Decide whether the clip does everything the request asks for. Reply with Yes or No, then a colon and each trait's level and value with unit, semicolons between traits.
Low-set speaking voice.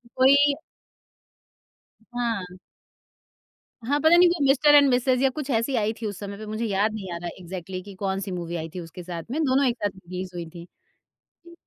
No: high, 215 Hz